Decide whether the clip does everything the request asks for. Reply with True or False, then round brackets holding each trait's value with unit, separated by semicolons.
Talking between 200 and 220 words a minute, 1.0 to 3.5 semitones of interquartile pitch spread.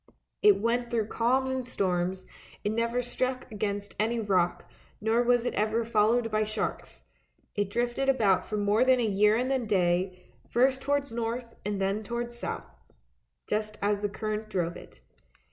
False (165 wpm; 2.9 semitones)